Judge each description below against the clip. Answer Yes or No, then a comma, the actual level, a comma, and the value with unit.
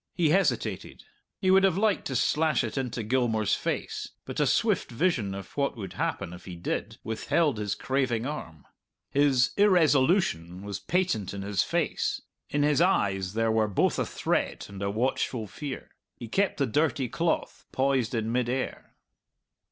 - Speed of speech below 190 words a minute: Yes, average, 165 wpm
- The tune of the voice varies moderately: No, wide, 6.5 semitones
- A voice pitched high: No, low, 125 Hz